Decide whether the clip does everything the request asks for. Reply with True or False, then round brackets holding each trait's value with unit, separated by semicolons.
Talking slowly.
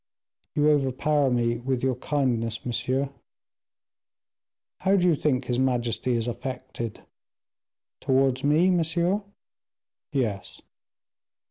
True (100 wpm)